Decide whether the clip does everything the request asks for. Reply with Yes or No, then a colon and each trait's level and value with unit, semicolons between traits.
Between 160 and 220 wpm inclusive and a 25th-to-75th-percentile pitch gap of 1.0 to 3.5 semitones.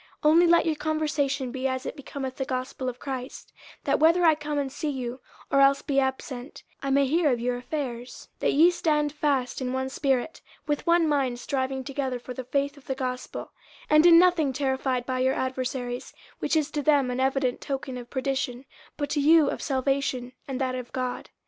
Yes: fast, 205 wpm; narrow, 2.5 semitones